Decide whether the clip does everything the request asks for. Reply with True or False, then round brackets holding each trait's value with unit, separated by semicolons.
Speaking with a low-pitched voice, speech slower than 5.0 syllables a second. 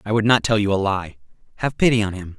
False (105 Hz; 6.6 syllables/s)